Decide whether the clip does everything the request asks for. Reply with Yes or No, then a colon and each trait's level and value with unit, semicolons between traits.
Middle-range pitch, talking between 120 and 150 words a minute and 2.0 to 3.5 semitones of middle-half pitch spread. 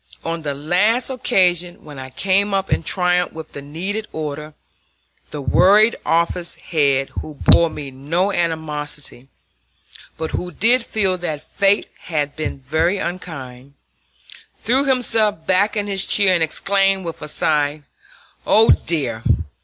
No: medium, 170 Hz; average, 140 wpm; average, 4.7 semitones